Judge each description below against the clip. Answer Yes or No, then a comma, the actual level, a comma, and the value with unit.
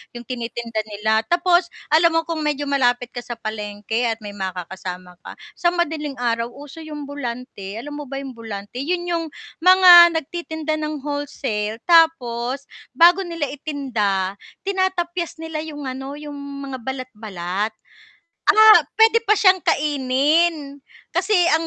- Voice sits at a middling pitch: No, very high, 280 Hz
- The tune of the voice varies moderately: No, wide, 6.0 semitones